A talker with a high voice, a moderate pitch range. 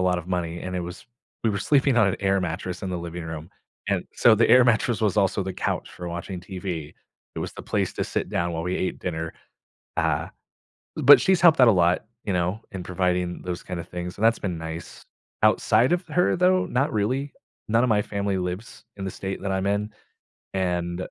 No: very low, 95 Hz; average, 3.8 semitones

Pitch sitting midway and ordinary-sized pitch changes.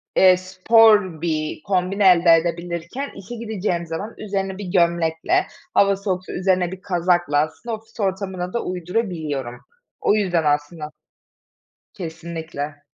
Yes: medium, 180 Hz; average, 3.2 semitones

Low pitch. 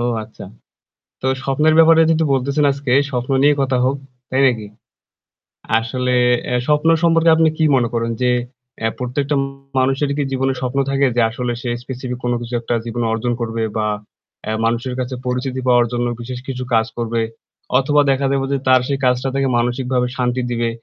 Yes: low, 130 Hz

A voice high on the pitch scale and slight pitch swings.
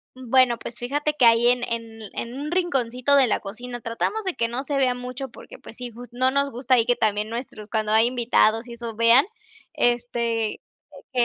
Yes: high, 245 Hz; narrow, 1.9 semitones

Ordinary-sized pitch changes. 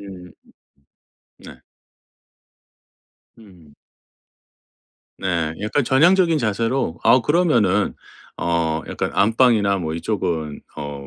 No: wide, 6.1 semitones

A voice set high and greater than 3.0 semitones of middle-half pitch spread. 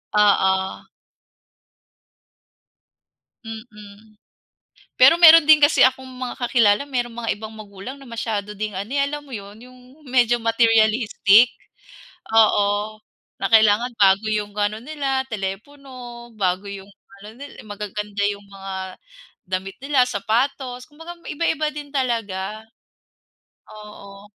Yes: high, 220 Hz; average, 4.1 semitones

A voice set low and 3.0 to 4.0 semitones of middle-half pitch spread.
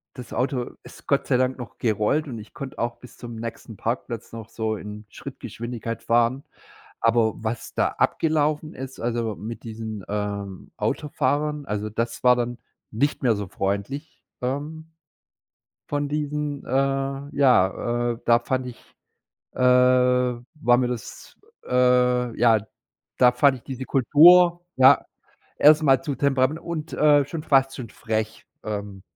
Yes: low, 125 Hz; average, 3.7 semitones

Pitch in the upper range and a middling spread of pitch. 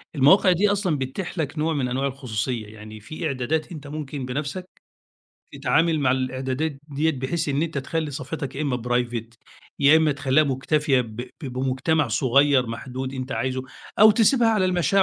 No: medium, 140 Hz; average, 3.7 semitones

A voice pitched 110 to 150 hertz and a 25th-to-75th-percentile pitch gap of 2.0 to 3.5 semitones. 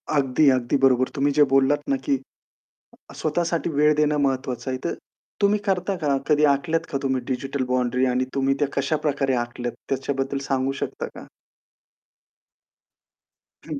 Yes: medium, 140 Hz; narrow, 2.5 semitones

